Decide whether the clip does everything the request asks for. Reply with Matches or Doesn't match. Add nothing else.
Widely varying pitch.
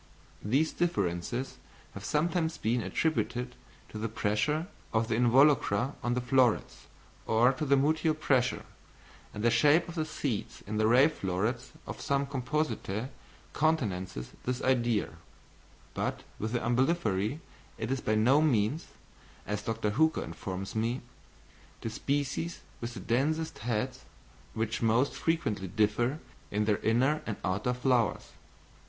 Doesn't match